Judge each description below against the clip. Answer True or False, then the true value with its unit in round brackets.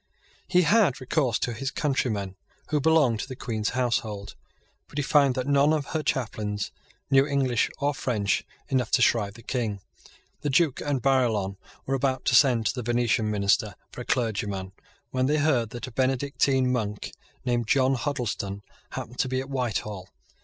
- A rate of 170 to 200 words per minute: True (175 wpm)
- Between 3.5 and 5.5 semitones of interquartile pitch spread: True (3.9 semitones)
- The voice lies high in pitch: False (125 Hz)